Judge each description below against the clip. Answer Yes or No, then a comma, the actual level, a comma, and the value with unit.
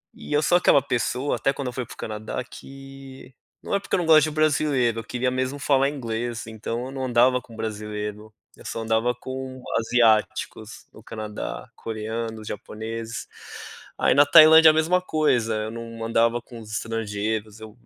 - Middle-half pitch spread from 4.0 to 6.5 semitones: No, average, 3.6 semitones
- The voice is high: No, low, 120 Hz